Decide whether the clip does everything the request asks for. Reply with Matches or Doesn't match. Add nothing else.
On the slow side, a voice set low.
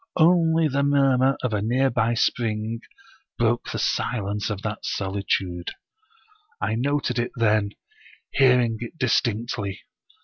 Matches